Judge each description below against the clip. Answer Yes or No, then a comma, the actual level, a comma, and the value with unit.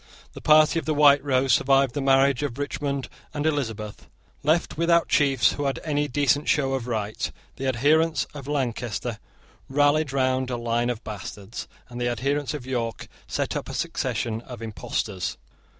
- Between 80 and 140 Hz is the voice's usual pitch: Yes, low, 135 Hz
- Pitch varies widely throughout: No, average, 3.4 semitones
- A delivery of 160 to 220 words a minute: Yes, average, 165 wpm